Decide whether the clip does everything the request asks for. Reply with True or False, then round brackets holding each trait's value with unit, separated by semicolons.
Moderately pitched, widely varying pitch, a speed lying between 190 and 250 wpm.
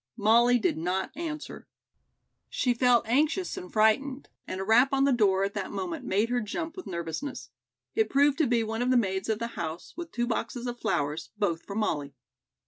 False (235 Hz; 5.9 semitones; 200 wpm)